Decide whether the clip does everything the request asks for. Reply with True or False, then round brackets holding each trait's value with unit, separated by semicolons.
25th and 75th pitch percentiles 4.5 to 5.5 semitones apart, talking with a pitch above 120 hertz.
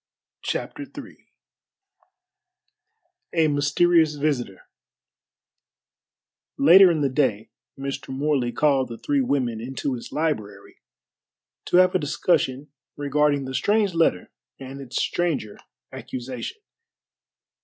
False (3.7 semitones; 140 Hz)